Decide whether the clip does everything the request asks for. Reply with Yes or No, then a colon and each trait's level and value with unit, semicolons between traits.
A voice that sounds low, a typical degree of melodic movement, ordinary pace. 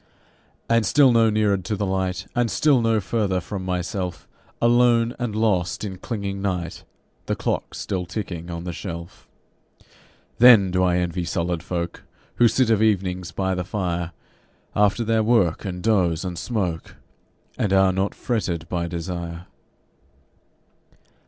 Yes: very low, 95 Hz; average, 3.8 semitones; average, 145 wpm